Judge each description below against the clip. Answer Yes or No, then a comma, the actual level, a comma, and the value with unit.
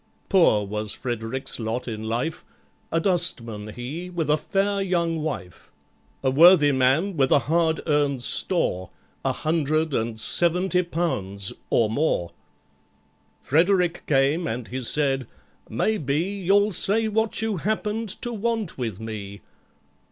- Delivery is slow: Yes, slow, 130 wpm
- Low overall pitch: No, medium, 155 Hz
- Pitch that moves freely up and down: Yes, wide, 7.4 semitones